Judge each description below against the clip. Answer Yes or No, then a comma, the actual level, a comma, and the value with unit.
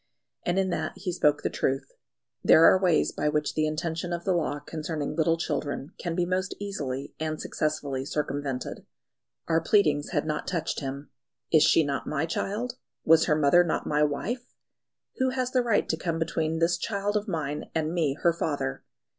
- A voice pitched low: No, medium, 160 Hz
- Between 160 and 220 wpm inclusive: Yes, average, 185 wpm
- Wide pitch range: No, average, 3.2 semitones